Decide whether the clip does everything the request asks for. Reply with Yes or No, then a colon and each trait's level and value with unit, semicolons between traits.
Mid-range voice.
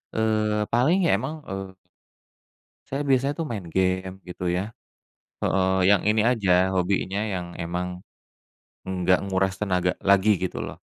No: very low, 95 Hz